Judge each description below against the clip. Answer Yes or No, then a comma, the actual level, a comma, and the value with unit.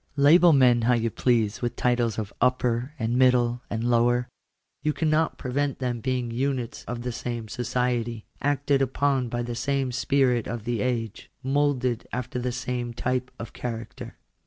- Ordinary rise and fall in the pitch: No, narrow, 1.8 semitones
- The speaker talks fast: No, average, 165 wpm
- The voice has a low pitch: Yes, low, 125 Hz